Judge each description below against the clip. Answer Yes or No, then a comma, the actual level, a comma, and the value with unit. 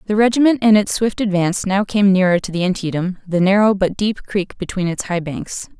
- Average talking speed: No, fast, 220 wpm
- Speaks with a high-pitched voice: Yes, high, 195 Hz